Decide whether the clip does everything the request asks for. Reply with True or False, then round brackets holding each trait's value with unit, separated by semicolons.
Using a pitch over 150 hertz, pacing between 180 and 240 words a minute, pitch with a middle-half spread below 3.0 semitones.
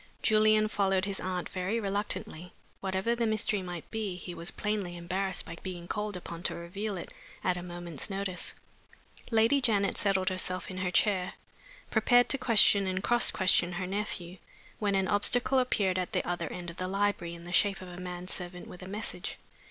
True (190 Hz; 190 wpm; 2.6 semitones)